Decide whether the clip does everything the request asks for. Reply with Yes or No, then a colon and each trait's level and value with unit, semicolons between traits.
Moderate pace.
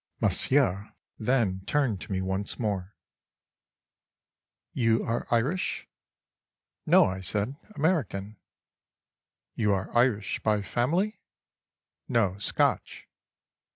No: slow, 80 wpm